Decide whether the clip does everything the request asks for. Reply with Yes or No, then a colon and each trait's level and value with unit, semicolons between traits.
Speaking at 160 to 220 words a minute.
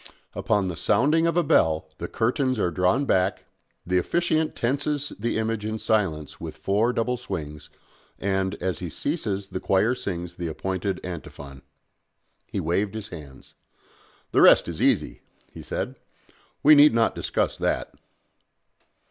No: average, 150 wpm